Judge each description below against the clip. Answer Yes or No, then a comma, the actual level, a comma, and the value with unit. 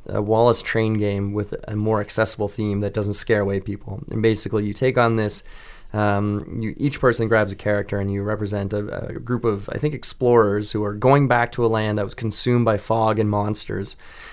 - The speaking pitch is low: Yes, low, 105 Hz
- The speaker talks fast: Yes, fast, 215 wpm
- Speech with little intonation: Yes, narrow, 1.9 semitones